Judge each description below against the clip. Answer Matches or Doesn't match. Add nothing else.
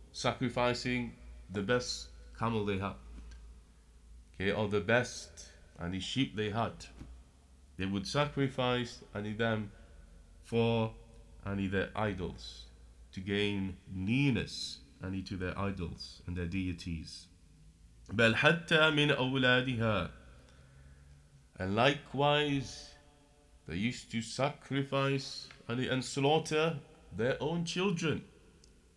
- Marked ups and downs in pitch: Matches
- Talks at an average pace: Doesn't match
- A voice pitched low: Matches